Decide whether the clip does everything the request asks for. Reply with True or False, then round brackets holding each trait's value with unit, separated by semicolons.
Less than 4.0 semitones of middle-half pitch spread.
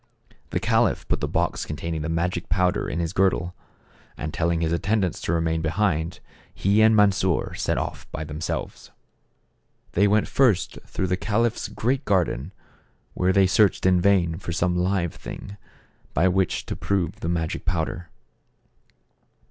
True (3.0 semitones)